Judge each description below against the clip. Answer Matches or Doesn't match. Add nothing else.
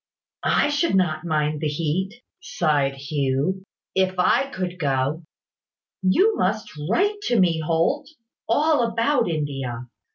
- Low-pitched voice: Doesn't match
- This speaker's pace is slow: Matches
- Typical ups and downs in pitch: Doesn't match